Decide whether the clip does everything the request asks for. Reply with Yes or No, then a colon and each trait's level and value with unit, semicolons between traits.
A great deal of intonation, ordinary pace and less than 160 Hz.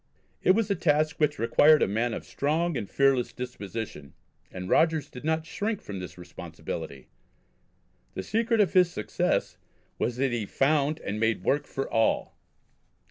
Yes: wide, 6.2 semitones; average, 160 wpm; low, 135 Hz